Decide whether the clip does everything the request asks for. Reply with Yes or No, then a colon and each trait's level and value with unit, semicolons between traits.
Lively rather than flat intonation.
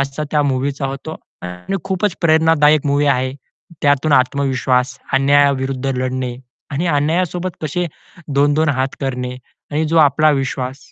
No: average, 2.9 semitones